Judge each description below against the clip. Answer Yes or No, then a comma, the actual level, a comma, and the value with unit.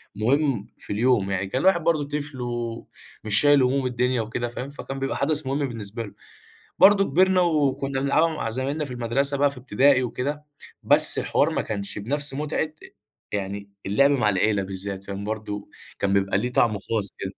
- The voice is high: No, low, 125 Hz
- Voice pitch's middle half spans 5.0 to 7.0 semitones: Yes, average, 5.3 semitones